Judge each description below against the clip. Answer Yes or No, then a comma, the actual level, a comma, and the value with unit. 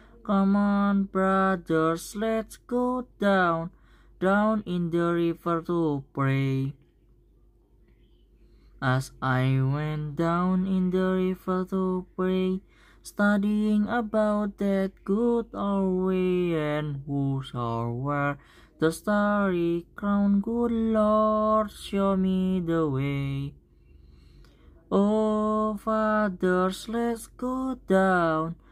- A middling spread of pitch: Yes, average, 4.8 semitones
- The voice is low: No, medium, 185 Hz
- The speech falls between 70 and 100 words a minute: Yes, average, 95 wpm